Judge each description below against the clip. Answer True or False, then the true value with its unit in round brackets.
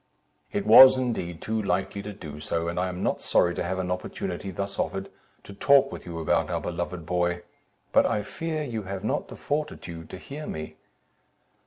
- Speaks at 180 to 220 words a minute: True (195 wpm)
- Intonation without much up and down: False (4.2 semitones)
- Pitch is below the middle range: True (95 Hz)